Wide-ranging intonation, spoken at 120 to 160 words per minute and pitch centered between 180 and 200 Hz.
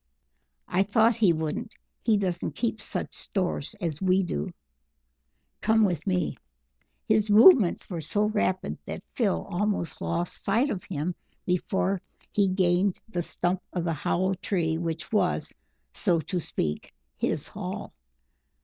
No: average, 3.2 semitones; average, 140 wpm; medium, 185 Hz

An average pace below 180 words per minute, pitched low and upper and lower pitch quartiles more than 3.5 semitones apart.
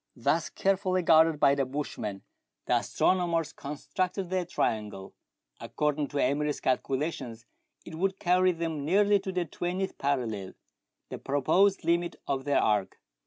No: average, 140 wpm; medium, 160 Hz; average, 4.8 semitones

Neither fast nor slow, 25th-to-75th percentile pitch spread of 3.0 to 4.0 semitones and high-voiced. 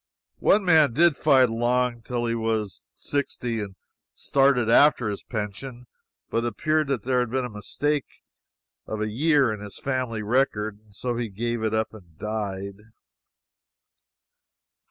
No: average, 155 wpm; average, 3.6 semitones; low, 120 Hz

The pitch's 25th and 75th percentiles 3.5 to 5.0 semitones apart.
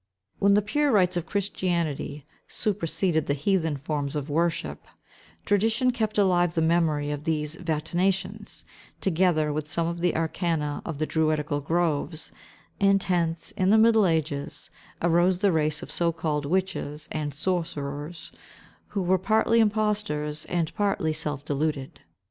Yes: average, 3.9 semitones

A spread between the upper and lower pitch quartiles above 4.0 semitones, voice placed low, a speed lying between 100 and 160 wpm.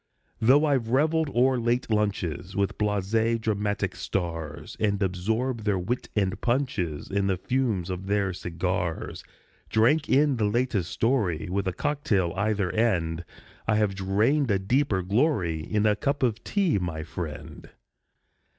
Yes: average, 4.8 semitones; low, 105 Hz; average, 150 wpm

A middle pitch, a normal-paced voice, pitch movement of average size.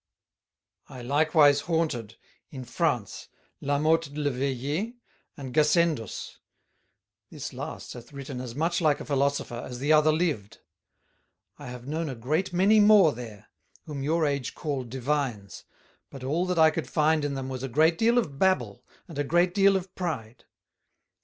Yes: medium, 145 Hz; average, 160 wpm; average, 4.2 semitones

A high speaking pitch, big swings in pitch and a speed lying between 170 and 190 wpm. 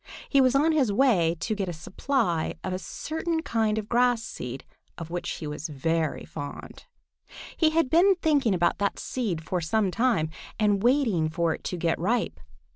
Yes: high, 210 Hz; wide, 7.6 semitones; average, 185 wpm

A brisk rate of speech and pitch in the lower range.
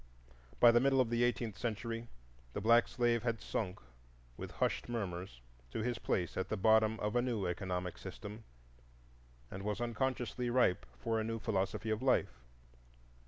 No: average, 165 wpm; low, 110 Hz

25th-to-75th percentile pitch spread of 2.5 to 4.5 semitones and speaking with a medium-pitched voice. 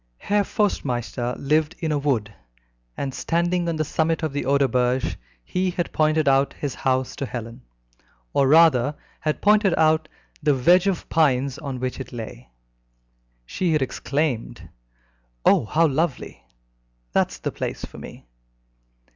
Yes: average, 4.1 semitones; medium, 145 Hz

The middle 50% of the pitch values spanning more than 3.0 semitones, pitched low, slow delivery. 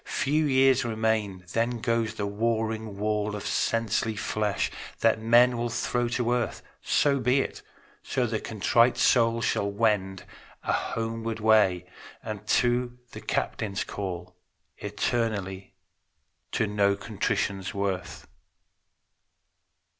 No: narrow, 2.6 semitones; low, 110 Hz; slow, 115 wpm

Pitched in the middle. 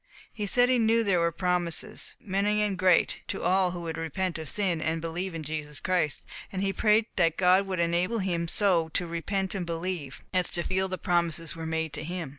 Yes: medium, 180 Hz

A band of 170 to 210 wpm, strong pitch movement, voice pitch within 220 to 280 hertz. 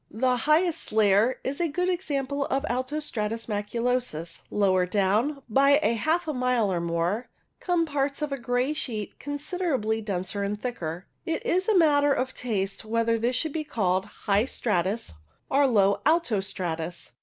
No: average, 160 wpm; wide, 5.9 semitones; high, 245 Hz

